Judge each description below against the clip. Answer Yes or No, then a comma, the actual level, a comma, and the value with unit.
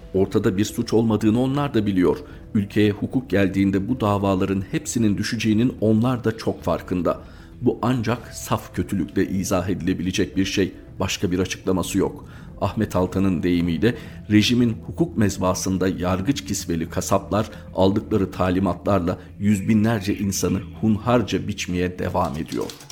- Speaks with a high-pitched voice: No, low, 100 Hz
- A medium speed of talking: Yes, average, 125 wpm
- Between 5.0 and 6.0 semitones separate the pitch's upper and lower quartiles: No, average, 3.0 semitones